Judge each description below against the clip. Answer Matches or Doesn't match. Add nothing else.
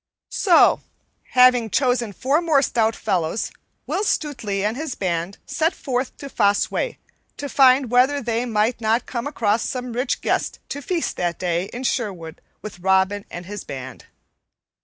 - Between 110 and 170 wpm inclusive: Matches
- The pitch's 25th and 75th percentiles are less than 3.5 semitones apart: Doesn't match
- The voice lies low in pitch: Doesn't match